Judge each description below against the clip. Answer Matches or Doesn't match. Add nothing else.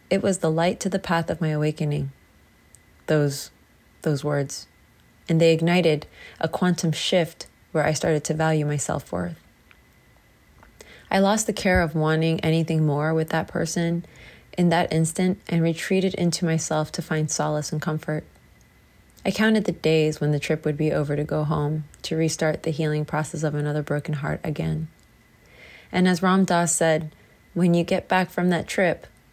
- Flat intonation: Matches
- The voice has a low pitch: Doesn't match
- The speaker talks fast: Doesn't match